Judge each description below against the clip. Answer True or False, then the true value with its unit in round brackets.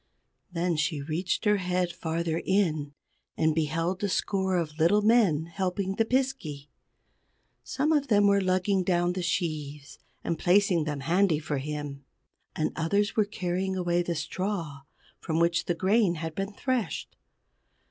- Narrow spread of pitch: False (3.9 semitones)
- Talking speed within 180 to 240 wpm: False (150 wpm)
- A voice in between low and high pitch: True (175 Hz)